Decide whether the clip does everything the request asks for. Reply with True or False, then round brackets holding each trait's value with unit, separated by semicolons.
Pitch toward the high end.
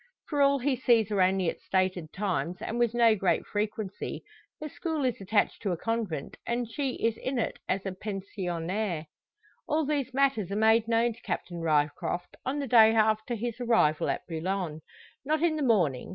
True (220 Hz)